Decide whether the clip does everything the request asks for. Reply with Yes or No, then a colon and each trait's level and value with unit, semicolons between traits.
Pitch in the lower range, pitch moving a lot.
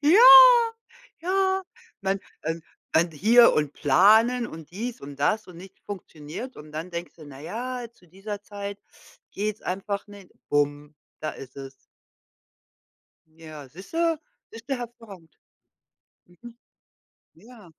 No: high, 195 Hz; wide, 7.1 semitones